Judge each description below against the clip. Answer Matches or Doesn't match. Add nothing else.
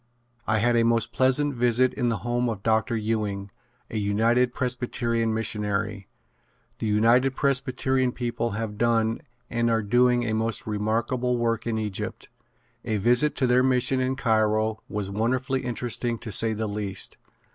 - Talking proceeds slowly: Doesn't match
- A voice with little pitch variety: Matches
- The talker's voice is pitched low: Matches